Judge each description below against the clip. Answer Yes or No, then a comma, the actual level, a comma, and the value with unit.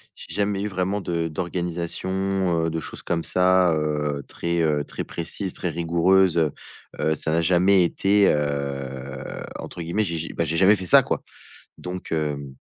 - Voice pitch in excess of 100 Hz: No, very low, 85 Hz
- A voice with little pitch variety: No, average, 3.2 semitones